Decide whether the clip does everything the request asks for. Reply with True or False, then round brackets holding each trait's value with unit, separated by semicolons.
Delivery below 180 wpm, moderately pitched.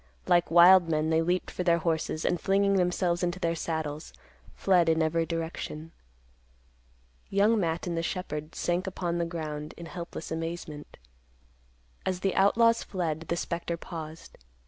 True (150 wpm; 170 Hz)